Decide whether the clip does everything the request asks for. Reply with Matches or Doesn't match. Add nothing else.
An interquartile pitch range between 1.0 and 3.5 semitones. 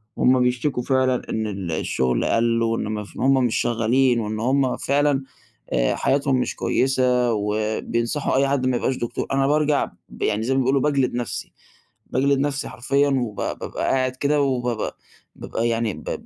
Matches